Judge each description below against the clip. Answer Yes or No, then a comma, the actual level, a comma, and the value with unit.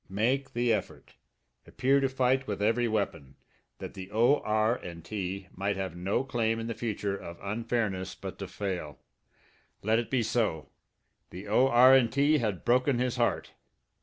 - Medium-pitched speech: No, low, 110 Hz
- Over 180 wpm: No, average, 165 wpm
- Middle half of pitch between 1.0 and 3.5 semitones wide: No, average, 4.0 semitones